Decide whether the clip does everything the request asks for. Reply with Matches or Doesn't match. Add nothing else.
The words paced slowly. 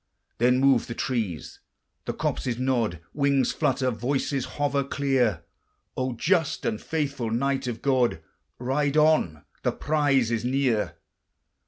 Matches